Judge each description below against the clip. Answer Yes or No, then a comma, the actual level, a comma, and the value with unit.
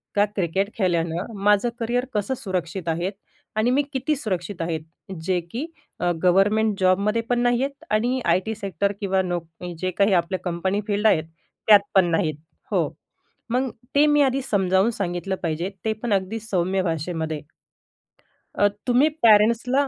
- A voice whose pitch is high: Yes, high, 200 Hz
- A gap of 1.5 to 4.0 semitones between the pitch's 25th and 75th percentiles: No, average, 4.4 semitones